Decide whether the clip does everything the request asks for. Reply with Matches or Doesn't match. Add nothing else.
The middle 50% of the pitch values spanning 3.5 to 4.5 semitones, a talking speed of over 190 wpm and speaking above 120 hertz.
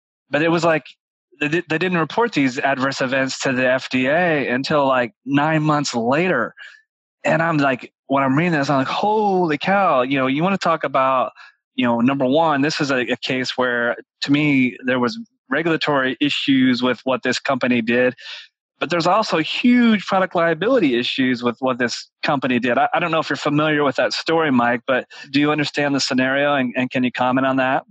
Matches